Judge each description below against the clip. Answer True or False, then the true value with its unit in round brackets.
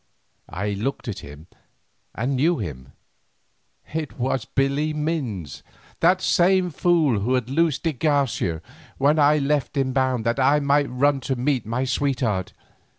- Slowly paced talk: False (150 wpm)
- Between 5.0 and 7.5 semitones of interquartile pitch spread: False (4.3 semitones)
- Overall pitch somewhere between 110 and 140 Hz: True (135 Hz)